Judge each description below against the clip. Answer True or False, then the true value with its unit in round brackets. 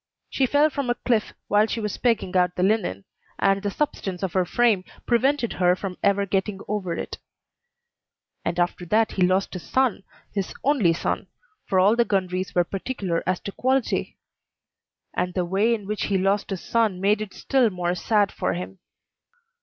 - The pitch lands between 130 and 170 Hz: False (195 Hz)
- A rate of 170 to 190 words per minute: True (185 wpm)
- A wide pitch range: False (3.7 semitones)